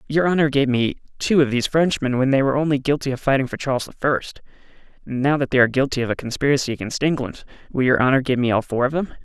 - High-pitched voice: No, low, 135 Hz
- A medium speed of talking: No, fast, 245 wpm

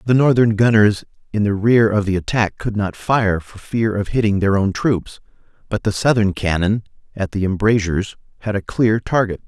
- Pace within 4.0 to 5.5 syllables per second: Yes, 5.0 syllables/s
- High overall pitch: No, low, 105 Hz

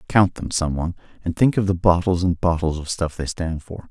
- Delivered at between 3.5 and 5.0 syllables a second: No, 5.5 syllables/s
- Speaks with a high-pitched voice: No, very low, 85 Hz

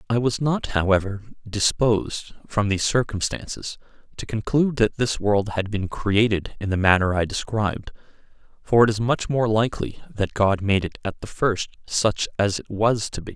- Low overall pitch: Yes, low, 110 Hz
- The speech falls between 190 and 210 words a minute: No, average, 180 wpm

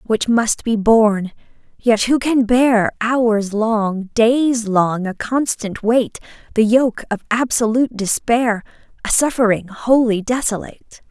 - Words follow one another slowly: Yes, slow, 130 wpm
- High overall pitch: Yes, high, 225 Hz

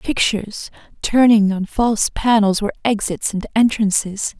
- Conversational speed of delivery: No, slow, 125 wpm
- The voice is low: No, high, 215 Hz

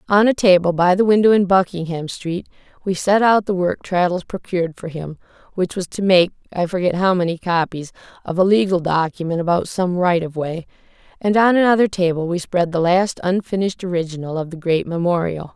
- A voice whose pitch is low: No, medium, 180 Hz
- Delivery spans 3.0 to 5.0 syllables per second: No, 5.6 syllables/s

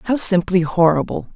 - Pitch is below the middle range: No, medium, 185 Hz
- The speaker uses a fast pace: No, slow, 135 wpm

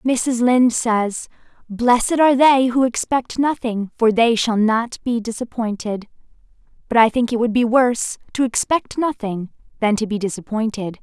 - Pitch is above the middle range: Yes, high, 235 Hz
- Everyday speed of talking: Yes, average, 160 wpm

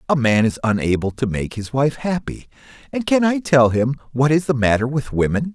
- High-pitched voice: No, low, 130 Hz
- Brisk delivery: Yes, fast, 215 wpm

